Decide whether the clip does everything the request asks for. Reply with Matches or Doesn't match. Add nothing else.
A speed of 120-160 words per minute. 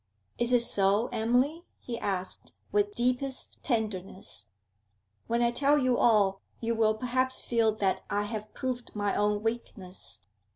Matches